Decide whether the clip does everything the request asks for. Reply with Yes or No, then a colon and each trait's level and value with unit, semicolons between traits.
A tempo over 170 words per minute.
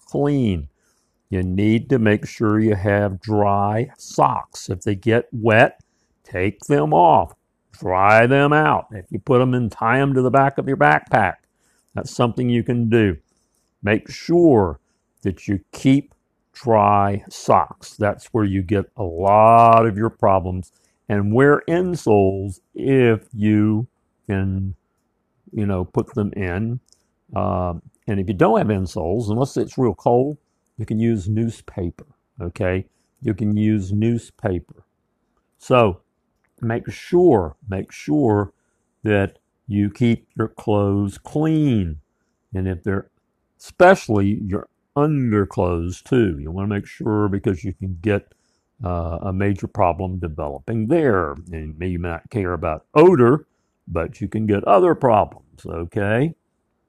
No: average, 140 wpm